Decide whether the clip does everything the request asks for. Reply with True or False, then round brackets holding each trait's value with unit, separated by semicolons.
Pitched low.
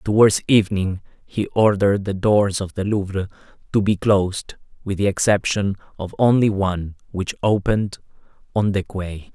True (100 Hz)